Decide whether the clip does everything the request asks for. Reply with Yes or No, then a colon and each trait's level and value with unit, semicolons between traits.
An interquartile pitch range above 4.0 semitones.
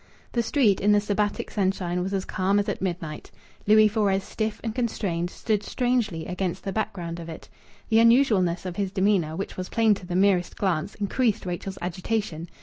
No: average, 3.2 semitones